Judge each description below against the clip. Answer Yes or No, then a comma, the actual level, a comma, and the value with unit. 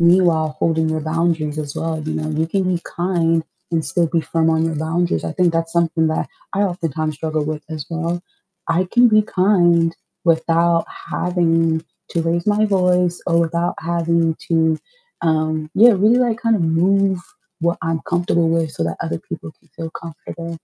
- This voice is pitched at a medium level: Yes, medium, 165 Hz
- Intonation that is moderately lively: No, narrow, 1.7 semitones